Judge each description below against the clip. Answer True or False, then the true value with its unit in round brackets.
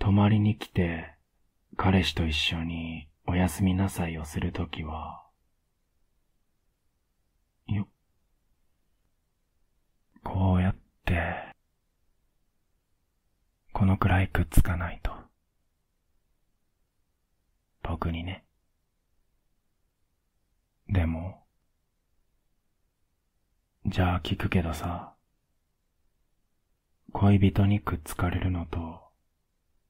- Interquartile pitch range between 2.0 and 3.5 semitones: True (2.8 semitones)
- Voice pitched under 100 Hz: True (90 Hz)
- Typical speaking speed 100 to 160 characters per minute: True (135 characters per minute)